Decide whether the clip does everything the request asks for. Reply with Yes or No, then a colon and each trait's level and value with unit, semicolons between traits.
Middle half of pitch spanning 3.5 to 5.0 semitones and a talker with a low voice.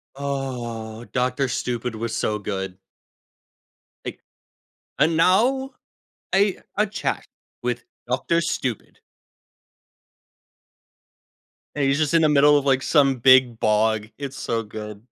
Yes: average, 4.5 semitones; low, 130 Hz